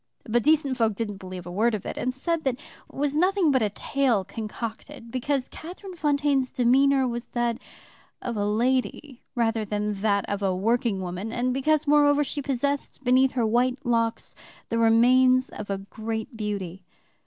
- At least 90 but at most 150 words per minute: No, average, 165 wpm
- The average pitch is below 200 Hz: No, high, 240 Hz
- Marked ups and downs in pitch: No, average, 4.1 semitones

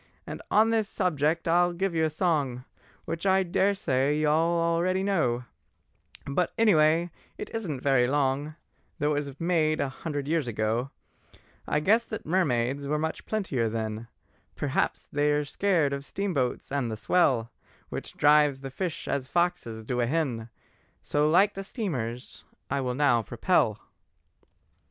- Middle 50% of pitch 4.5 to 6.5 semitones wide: Yes, average, 4.9 semitones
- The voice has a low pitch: No, medium, 150 Hz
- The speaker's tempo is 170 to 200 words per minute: No, average, 150 wpm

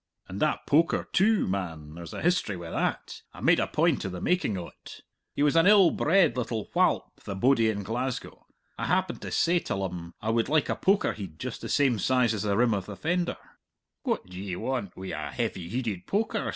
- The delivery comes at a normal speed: No, fast, 215 wpm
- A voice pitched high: No, low, 115 Hz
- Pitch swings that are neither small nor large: No, wide, 8.7 semitones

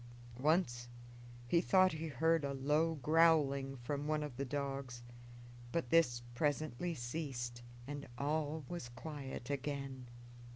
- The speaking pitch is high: No, medium, 145 Hz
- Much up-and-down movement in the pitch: No, average, 3.3 semitones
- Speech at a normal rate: No, slow, 125 wpm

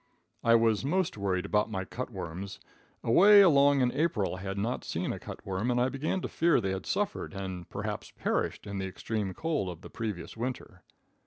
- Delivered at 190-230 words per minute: Yes, average, 195 wpm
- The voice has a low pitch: Yes, low, 110 Hz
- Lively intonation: Yes, wide, 6.2 semitones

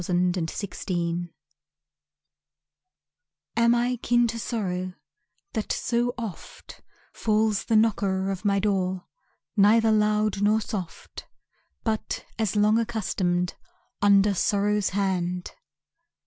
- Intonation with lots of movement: No, average, 3.0 semitones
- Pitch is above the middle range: Yes, high, 205 Hz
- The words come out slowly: Yes, slow, 105 wpm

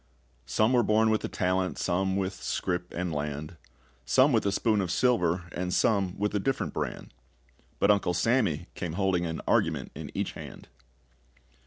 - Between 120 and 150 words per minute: No, average, 170 wpm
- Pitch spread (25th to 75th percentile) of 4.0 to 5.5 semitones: No, average, 3.5 semitones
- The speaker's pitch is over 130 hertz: No, very low, 95 Hz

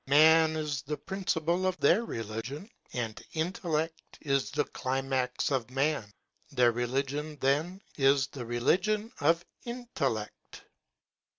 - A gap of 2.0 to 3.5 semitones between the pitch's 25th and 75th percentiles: No, average, 4.0 semitones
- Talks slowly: Yes, slow, 120 wpm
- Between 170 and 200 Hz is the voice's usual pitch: No, medium, 145 Hz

